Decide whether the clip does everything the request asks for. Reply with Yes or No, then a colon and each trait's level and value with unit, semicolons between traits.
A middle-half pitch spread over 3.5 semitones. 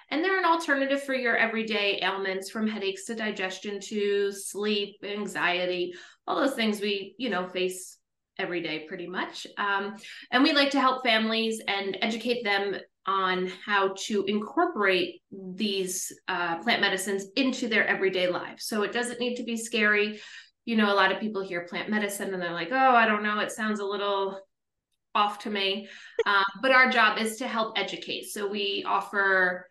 No: average, 3.0 semitones